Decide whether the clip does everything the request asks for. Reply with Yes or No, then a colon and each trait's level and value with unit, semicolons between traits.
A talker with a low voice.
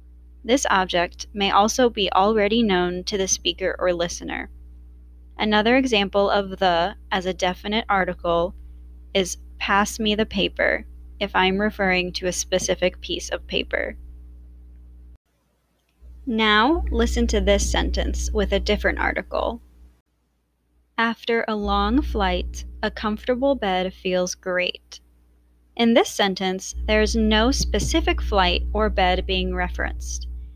No: medium, 185 Hz